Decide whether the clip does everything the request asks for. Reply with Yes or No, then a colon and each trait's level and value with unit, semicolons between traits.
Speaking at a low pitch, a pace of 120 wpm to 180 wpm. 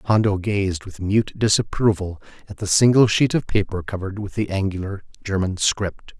Yes: low, 100 Hz; average, 165 wpm